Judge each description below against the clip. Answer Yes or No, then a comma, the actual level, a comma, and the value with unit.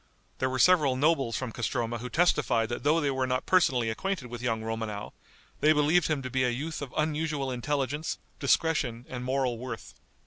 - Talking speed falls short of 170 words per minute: No, average, 185 wpm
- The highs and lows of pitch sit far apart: No, average, 4.0 semitones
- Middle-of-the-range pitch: No, low, 130 Hz